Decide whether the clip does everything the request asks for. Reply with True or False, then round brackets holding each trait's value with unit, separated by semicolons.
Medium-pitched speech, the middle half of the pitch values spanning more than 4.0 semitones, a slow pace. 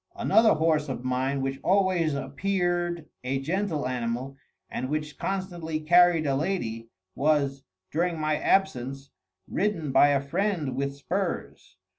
True (155 Hz; 4.6 semitones; 130 wpm)